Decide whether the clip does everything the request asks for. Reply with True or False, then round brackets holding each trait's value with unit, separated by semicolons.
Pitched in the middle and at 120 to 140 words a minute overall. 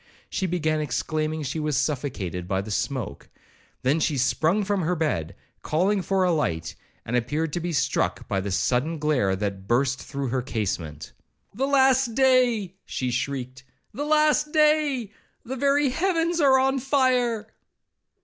False (160 Hz; 150 wpm)